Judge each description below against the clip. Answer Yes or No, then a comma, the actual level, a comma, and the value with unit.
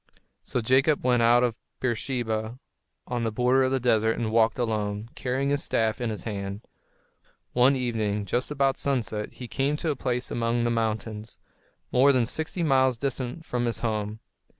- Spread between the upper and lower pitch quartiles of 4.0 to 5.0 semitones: No, average, 2.8 semitones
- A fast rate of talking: No, average, 175 wpm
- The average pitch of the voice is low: Yes, low, 120 Hz